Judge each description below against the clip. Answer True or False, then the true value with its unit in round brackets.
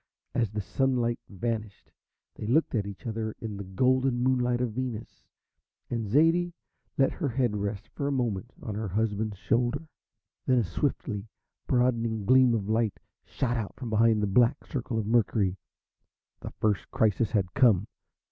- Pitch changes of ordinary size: True (3.3 semitones)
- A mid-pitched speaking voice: False (115 Hz)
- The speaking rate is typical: True (160 wpm)